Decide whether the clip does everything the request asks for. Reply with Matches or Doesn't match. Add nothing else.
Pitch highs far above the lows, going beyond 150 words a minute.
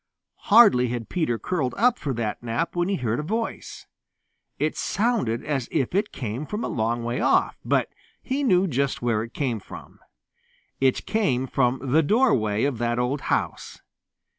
Matches